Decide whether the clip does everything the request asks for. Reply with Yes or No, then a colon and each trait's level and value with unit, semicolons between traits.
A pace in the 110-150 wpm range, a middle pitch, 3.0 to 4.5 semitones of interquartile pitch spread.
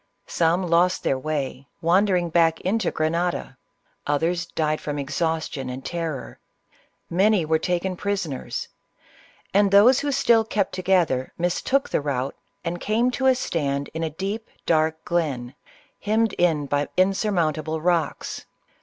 Yes: average, 140 wpm; medium, 170 Hz; average, 3.9 semitones